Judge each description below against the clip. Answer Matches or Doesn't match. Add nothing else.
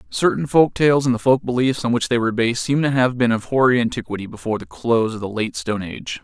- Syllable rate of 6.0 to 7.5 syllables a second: Matches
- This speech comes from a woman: Doesn't match